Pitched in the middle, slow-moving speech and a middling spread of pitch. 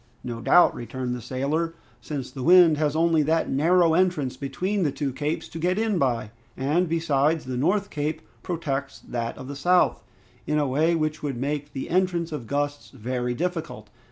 No: medium, 150 Hz; average, 185 wpm; average, 3.9 semitones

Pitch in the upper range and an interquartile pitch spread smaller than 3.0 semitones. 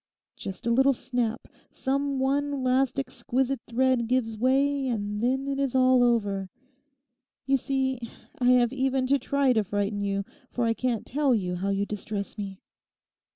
No: very high, 250 Hz; average, 3.7 semitones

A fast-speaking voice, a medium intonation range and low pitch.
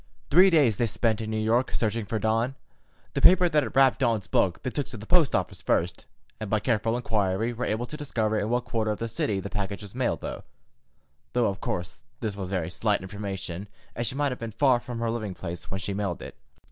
Yes: fast, 230 wpm; average, 3.5 semitones; low, 110 Hz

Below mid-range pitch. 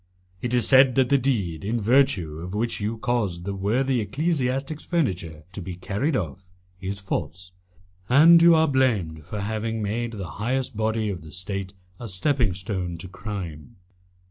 Yes: low, 105 Hz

